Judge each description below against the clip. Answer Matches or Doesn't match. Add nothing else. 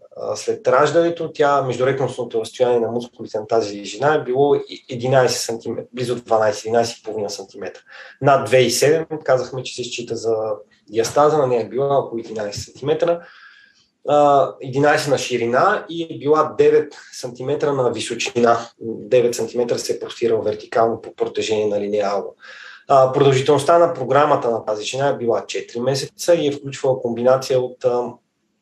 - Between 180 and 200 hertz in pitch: Doesn't match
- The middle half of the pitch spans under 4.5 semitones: Doesn't match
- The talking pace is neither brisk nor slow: Matches